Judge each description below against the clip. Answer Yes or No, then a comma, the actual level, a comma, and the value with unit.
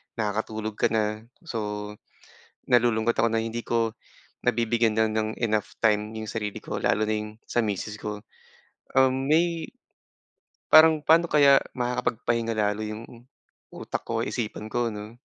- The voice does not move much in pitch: Yes, narrow, 2.2 semitones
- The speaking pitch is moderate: No, low, 110 Hz